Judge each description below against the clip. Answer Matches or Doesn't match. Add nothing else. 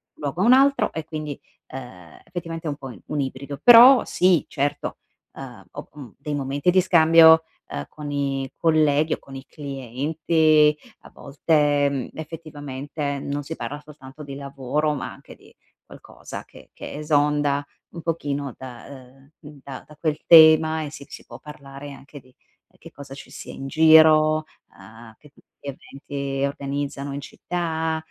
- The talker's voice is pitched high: Doesn't match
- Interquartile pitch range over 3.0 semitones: Doesn't match